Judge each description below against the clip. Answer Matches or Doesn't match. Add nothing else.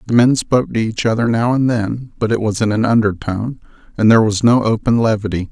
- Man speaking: Matches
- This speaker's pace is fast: Matches